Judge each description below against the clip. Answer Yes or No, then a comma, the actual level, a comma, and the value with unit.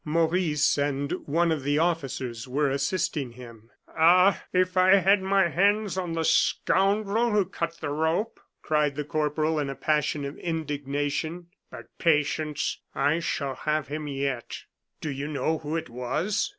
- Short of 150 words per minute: No, average, 155 wpm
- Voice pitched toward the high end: No, medium, 155 Hz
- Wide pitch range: No, average, 3.7 semitones